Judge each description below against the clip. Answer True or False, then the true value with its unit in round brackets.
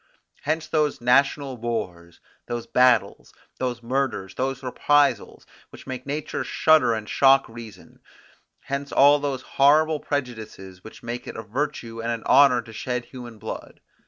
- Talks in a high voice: False (125 Hz)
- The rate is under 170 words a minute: True (145 wpm)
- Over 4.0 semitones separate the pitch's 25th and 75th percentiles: False (3.4 semitones)